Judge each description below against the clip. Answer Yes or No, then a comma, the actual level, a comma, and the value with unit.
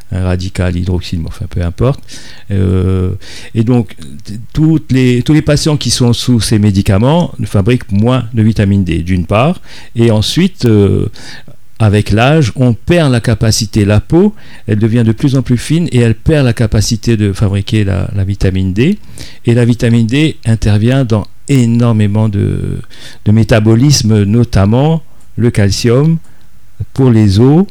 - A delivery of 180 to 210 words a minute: No, average, 155 wpm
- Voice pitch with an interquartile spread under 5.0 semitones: Yes, average, 3.6 semitones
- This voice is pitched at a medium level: No, low, 115 Hz